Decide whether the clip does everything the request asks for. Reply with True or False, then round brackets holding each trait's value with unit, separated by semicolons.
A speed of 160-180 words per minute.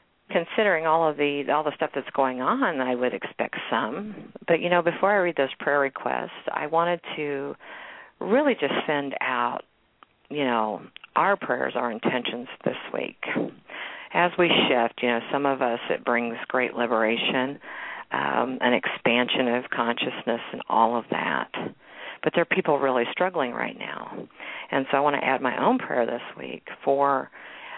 True (170 wpm)